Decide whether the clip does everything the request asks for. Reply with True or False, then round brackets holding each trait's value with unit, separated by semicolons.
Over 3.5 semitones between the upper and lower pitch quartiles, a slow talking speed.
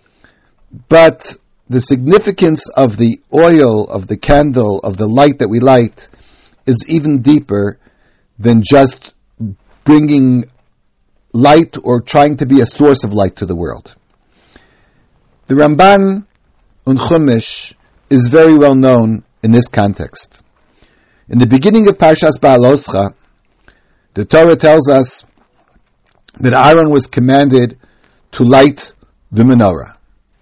True (5.1 semitones; 120 wpm)